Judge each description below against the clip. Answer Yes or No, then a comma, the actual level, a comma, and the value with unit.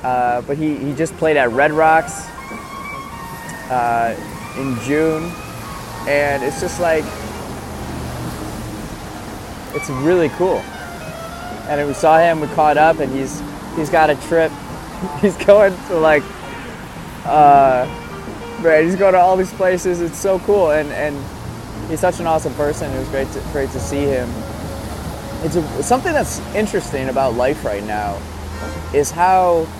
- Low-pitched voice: No, medium, 145 Hz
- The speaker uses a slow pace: No, average, 145 wpm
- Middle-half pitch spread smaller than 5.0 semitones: Yes, average, 4.6 semitones